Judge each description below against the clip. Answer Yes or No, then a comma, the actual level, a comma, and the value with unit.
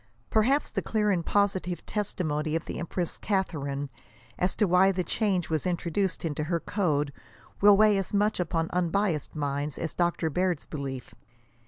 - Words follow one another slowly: No, average, 160 wpm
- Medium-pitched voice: Yes, medium, 175 Hz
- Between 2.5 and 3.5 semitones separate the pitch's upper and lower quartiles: No, average, 4.3 semitones